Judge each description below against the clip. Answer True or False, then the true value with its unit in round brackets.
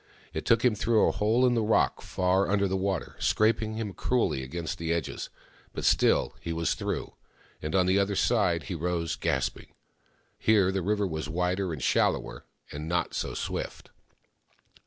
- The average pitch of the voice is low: True (95 Hz)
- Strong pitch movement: False (4.2 semitones)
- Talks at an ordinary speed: True (175 wpm)